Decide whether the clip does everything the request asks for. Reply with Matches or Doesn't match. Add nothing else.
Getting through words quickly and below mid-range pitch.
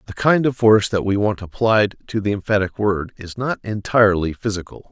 Doesn't match